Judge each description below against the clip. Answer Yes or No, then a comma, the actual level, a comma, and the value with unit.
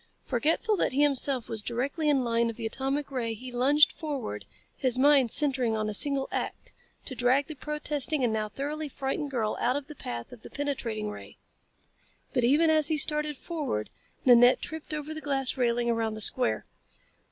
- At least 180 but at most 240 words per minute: Yes, average, 185 wpm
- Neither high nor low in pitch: No, very high, 270 Hz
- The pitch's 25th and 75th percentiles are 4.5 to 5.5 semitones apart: No, average, 3.9 semitones